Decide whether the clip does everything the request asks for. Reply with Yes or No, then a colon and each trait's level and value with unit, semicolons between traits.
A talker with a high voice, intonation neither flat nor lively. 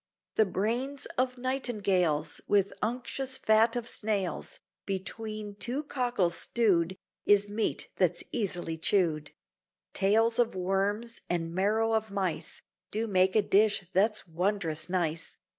Yes: high, 205 Hz; average, 3.6 semitones